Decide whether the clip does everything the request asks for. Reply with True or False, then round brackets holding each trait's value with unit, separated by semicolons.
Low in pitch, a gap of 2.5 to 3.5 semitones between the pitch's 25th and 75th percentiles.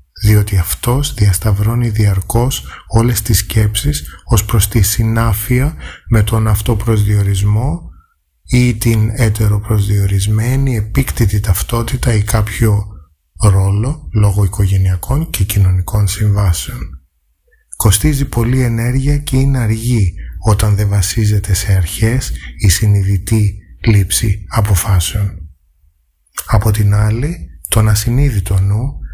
True (105 Hz; 3.1 semitones)